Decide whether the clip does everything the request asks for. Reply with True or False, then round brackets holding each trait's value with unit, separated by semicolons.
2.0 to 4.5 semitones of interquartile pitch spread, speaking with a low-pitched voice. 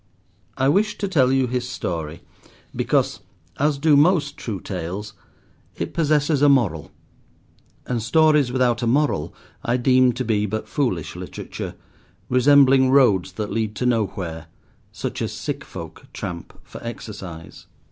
False (5.4 semitones; 125 Hz)